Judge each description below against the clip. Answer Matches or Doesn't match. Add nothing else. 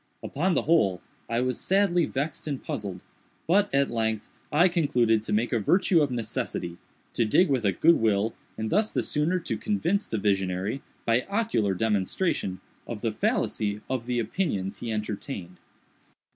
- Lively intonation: Matches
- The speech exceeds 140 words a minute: Matches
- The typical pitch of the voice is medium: Doesn't match